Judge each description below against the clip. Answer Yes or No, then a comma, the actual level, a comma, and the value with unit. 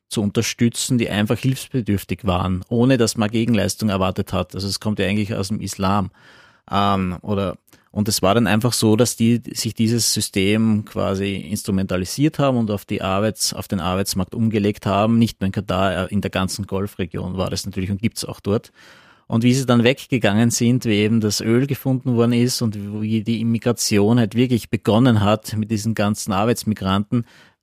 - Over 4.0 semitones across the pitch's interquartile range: No, average, 2.9 semitones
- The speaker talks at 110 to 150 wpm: No, average, 185 wpm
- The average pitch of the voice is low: Yes, low, 105 Hz